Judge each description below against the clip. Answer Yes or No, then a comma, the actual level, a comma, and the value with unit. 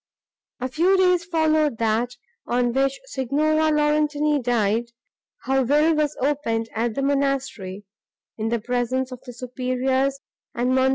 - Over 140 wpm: No, slow, 135 wpm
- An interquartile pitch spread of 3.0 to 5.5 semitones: Yes, average, 3.7 semitones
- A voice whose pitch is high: Yes, very high, 265 Hz